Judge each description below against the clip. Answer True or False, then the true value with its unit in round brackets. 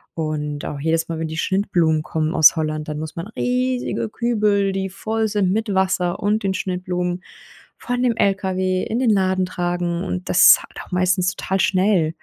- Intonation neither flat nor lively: True (3.4 semitones)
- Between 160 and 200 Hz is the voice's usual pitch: True (185 Hz)